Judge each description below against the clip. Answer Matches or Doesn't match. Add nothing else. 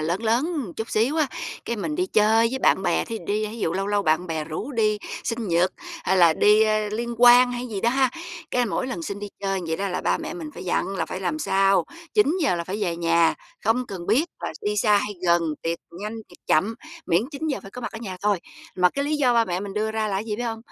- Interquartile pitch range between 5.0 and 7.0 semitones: Doesn't match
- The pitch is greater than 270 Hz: Doesn't match